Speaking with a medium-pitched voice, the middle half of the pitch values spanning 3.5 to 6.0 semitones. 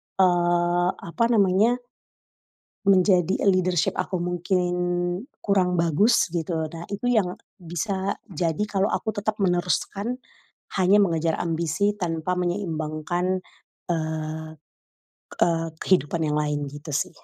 No: medium, 175 Hz; average, 2.8 semitones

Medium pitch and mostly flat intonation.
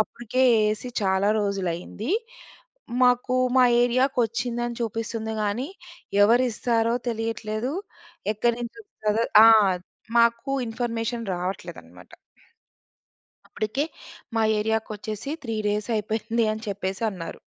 No: high, 225 Hz; narrow, 2.3 semitones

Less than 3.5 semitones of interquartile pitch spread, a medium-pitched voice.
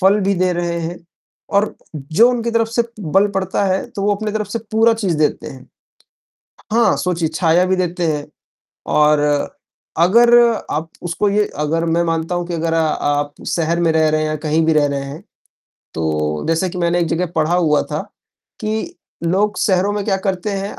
No: average, 4.0 semitones; medium, 175 Hz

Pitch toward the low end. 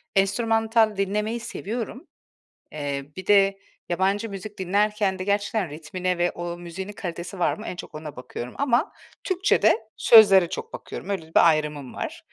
No: high, 195 Hz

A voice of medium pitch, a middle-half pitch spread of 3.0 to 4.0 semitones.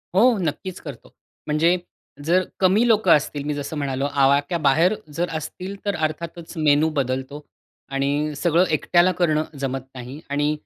Yes: medium, 155 Hz; average, 3.7 semitones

